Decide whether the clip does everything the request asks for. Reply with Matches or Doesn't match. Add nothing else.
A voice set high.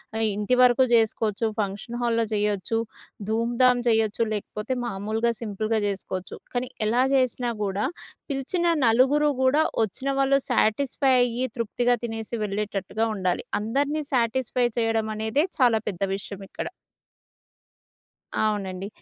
Matches